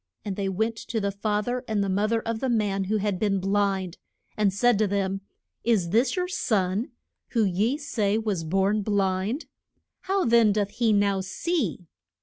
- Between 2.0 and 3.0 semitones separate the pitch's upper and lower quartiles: Yes, average, 2.7 semitones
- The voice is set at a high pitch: Yes, high, 205 Hz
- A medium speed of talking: Yes, average, 185 wpm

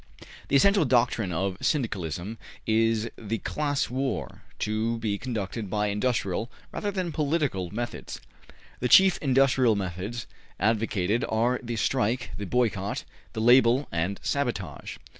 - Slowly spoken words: Yes, slow, 130 wpm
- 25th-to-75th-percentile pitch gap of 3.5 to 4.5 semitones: Yes, average, 4.1 semitones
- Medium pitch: No, low, 115 Hz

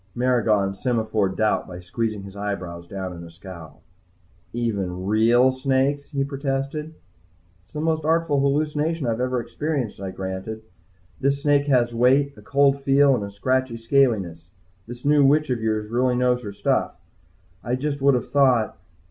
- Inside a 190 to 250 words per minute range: No, average, 160 wpm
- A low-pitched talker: Yes, low, 125 Hz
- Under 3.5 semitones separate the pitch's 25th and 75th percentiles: No, average, 5.2 semitones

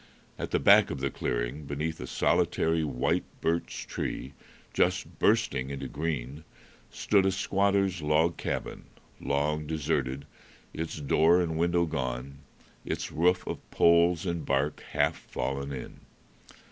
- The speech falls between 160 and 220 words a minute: No, slow, 135 wpm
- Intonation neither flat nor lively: Yes, average, 3.4 semitones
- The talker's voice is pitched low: Yes, very low, 75 Hz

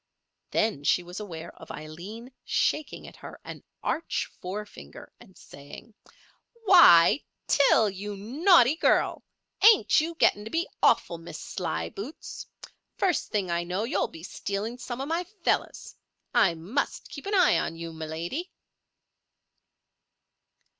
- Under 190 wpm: Yes, slow, 135 wpm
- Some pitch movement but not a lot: No, wide, 8.8 semitones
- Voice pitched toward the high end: Yes, high, 210 Hz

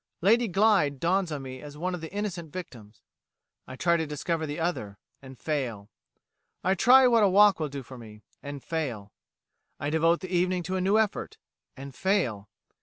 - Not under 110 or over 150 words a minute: No, average, 185 wpm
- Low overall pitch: No, medium, 165 Hz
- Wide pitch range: Yes, wide, 5.8 semitones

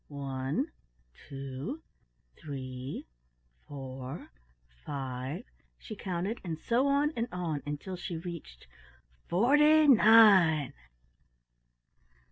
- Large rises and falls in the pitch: Yes, wide, 8.7 semitones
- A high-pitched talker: No, medium, 170 Hz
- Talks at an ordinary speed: No, slow, 85 wpm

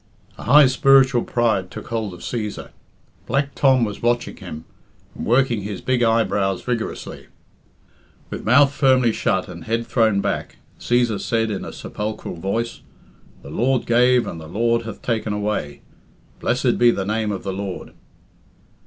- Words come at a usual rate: Yes, average, 155 wpm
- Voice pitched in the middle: No, low, 115 Hz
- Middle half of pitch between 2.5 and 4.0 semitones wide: Yes, average, 3.3 semitones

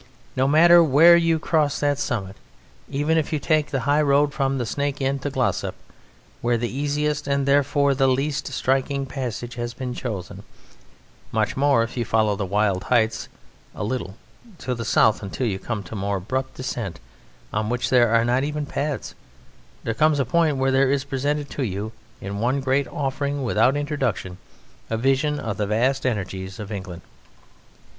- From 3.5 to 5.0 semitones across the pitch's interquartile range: Yes, average, 4.2 semitones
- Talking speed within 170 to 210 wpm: Yes, average, 180 wpm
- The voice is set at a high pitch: No, low, 130 Hz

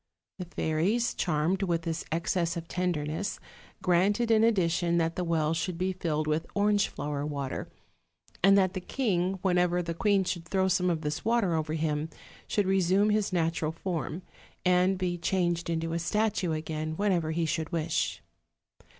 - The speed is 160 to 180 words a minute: Yes, average, 165 wpm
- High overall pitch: No, medium, 175 Hz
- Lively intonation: No, average, 2.9 semitones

